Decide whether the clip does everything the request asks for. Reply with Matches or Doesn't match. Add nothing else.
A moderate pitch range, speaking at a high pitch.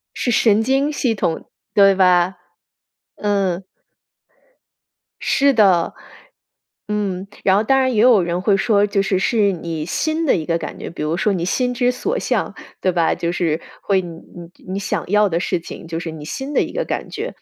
Matches